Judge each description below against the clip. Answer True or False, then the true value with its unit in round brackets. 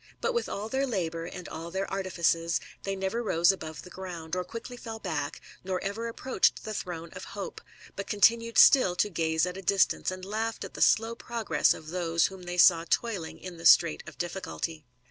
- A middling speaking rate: False (215 wpm)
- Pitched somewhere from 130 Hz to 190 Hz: True (185 Hz)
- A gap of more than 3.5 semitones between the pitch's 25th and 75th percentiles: True (4.4 semitones)